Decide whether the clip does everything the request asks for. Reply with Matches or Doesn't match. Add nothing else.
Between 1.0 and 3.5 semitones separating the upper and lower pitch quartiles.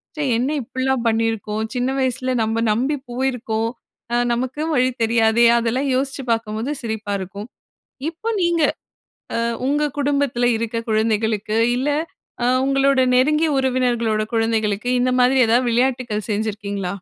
Matches